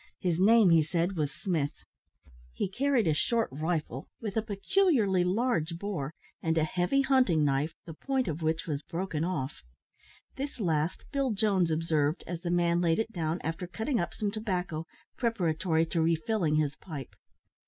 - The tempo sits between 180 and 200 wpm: No, average, 165 wpm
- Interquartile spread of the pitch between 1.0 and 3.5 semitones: No, average, 5.0 semitones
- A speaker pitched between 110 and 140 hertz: No, medium, 175 Hz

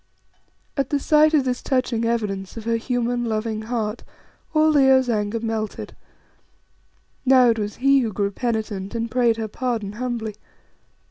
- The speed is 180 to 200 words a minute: No, average, 150 wpm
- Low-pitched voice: No, high, 230 Hz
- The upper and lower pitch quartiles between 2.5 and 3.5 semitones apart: Yes, average, 2.8 semitones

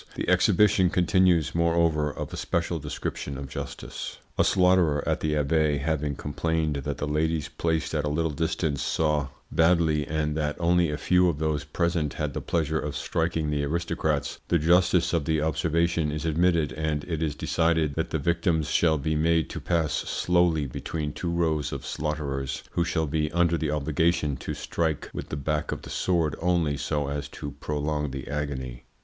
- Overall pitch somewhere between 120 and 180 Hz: No, very low, 80 Hz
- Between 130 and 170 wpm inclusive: No, average, 180 wpm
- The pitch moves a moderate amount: No, narrow, 2.2 semitones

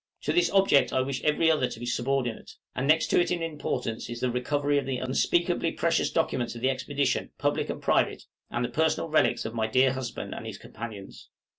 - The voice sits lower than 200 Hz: Yes, low, 135 Hz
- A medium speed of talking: No, fast, 210 wpm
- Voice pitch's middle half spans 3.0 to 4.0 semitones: No, average, 4.5 semitones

